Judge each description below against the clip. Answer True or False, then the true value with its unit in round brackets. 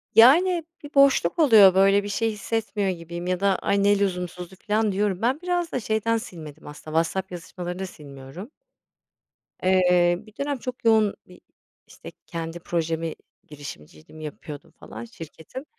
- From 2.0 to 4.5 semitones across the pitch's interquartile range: False (5.0 semitones)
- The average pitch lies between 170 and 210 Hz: True (190 Hz)